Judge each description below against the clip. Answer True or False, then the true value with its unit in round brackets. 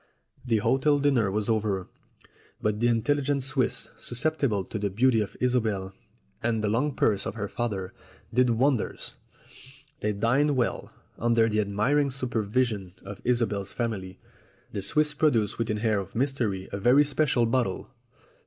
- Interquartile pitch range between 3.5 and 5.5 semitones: True (4.0 semitones)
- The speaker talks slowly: False (150 wpm)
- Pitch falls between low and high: False (115 Hz)